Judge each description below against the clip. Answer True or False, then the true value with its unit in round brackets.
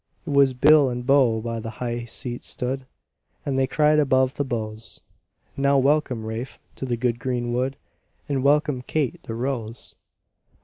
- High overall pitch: False (130 Hz)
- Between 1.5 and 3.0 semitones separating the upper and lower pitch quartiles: True (2.7 semitones)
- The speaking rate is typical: True (165 wpm)